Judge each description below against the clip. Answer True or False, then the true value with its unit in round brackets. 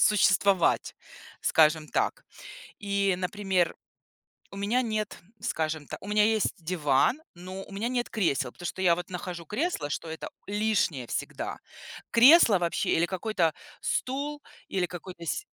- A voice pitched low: False (190 Hz)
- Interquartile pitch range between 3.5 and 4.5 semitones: True (4.2 semitones)